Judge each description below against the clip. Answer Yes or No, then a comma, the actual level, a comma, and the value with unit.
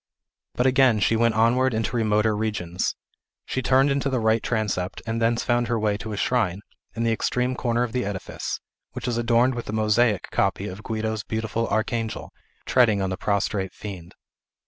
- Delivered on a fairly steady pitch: Yes, narrow, 2.3 semitones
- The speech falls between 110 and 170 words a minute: No, average, 185 wpm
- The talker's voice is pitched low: Yes, low, 110 Hz